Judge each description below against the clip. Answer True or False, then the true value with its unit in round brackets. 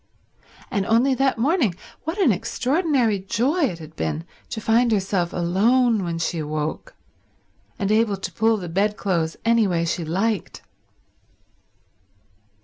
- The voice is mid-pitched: False (205 Hz)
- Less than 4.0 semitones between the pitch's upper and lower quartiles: False (5.6 semitones)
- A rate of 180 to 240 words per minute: False (140 wpm)